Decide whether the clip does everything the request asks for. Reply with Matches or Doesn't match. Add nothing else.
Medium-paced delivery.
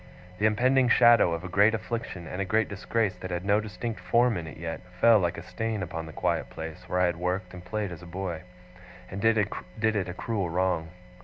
Doesn't match